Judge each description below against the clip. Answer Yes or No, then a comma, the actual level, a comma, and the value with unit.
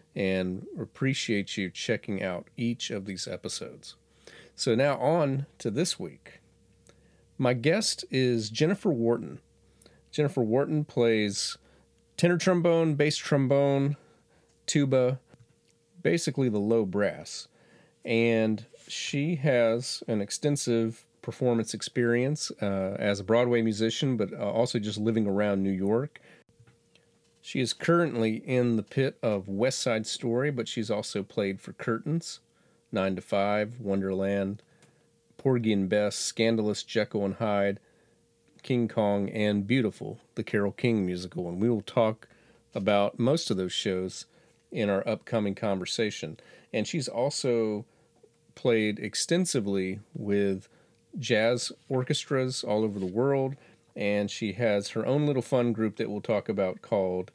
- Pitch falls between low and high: No, low, 115 Hz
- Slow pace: Yes, slow, 130 wpm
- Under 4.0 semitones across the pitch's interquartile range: No, average, 4.7 semitones